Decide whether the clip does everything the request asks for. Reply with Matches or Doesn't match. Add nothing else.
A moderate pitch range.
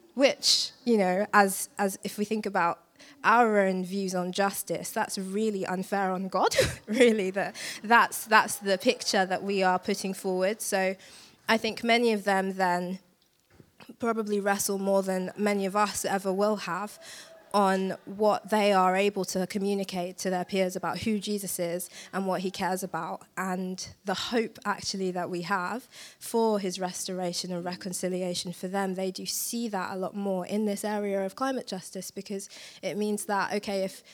Doesn't match